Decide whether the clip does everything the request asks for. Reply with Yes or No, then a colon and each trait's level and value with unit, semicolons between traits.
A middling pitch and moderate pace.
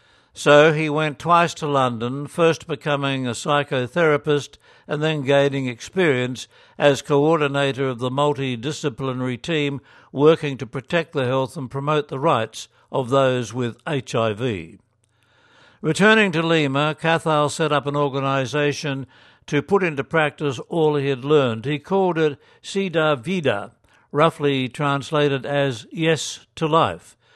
No: medium, 145 Hz; slow, 130 wpm